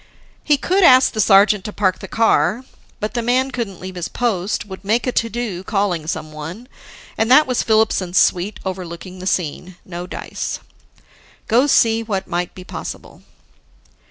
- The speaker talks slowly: No, average, 165 wpm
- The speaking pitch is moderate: No, high, 205 Hz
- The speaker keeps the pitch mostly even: No, average, 4.2 semitones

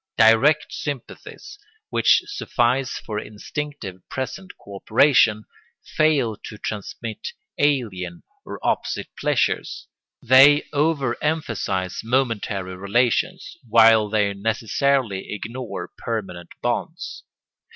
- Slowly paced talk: Yes, slow, 90 wpm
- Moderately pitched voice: No, low, 115 Hz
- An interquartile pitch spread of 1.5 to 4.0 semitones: No, average, 5.1 semitones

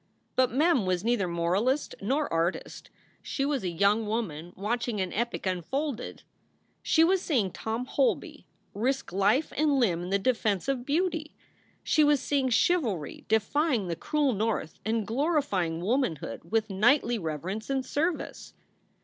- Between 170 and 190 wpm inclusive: No, average, 145 wpm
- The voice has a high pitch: Yes, high, 230 Hz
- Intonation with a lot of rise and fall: Yes, wide, 6.5 semitones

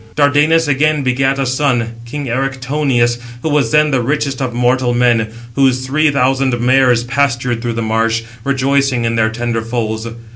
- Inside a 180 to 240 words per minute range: No, average, 160 wpm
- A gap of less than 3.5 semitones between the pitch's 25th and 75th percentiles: Yes, average, 2.7 semitones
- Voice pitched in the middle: No, low, 130 Hz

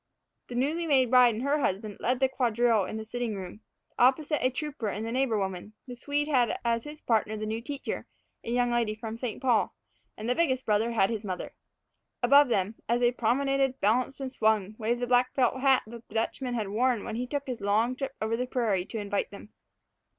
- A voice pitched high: Yes, high, 240 Hz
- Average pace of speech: No, fast, 215 wpm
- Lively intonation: No, average, 3.1 semitones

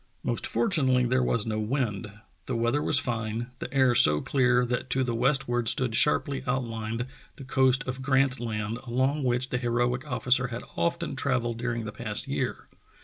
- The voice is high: No, low, 125 Hz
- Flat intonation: Yes, narrow, 2.2 semitones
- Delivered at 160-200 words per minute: Yes, average, 175 wpm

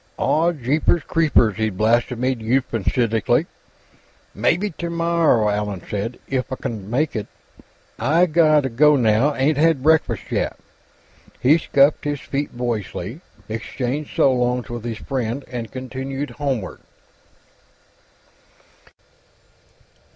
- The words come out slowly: Yes, slow, 110 wpm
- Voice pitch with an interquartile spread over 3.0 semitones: Yes, average, 4.6 semitones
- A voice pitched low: Yes, low, 130 Hz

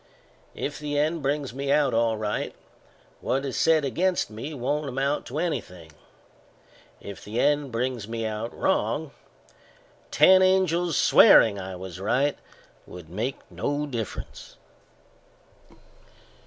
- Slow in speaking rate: Yes, slow, 125 wpm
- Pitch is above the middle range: No, low, 135 Hz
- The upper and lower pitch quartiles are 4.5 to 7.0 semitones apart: Yes, average, 5.1 semitones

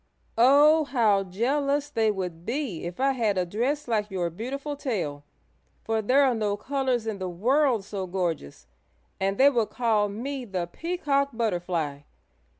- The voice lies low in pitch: No, high, 225 Hz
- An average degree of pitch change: No, wide, 6.4 semitones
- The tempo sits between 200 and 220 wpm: No, average, 155 wpm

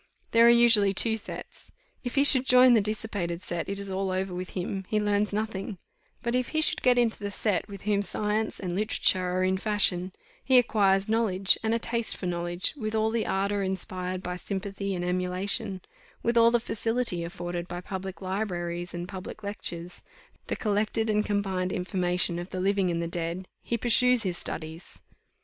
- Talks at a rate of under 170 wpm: No, average, 190 wpm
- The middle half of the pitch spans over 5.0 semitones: No, average, 3.3 semitones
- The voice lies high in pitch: Yes, high, 195 Hz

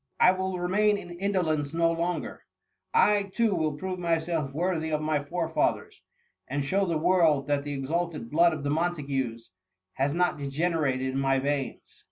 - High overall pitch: No, medium, 160 Hz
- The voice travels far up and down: No, average, 3.8 semitones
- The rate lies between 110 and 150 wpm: No, average, 165 wpm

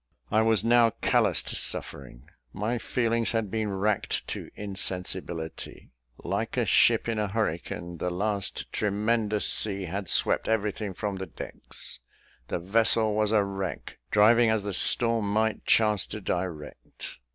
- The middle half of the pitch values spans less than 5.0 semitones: Yes, average, 2.7 semitones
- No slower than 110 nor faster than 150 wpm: Yes, average, 145 wpm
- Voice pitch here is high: No, low, 105 Hz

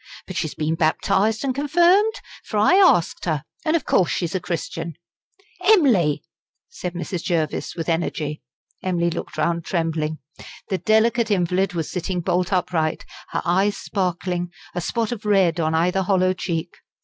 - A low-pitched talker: No, medium, 180 Hz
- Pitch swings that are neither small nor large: Yes, average, 3.9 semitones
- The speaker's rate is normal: Yes, average, 155 wpm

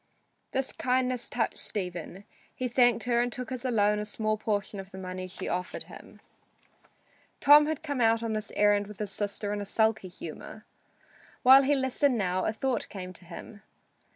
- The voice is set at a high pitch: Yes, high, 220 Hz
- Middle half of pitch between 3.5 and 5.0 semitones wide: Yes, average, 3.9 semitones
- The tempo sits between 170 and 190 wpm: Yes, average, 180 wpm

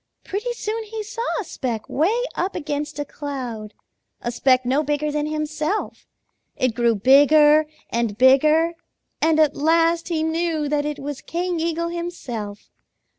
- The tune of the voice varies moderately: Yes, average, 4.0 semitones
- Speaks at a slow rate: No, average, 150 wpm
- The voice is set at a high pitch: Yes, very high, 300 Hz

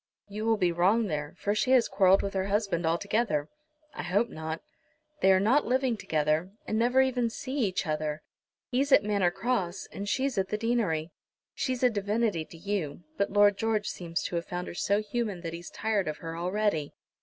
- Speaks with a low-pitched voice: No, high, 200 Hz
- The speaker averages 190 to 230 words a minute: Yes, average, 200 wpm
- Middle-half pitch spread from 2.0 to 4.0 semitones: No, average, 4.6 semitones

